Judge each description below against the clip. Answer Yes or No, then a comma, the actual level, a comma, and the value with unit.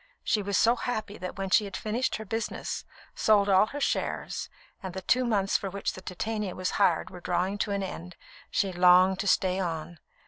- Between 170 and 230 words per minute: Yes, fast, 205 wpm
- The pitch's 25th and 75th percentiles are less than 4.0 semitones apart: Yes, narrow, 2.6 semitones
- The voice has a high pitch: Yes, high, 195 Hz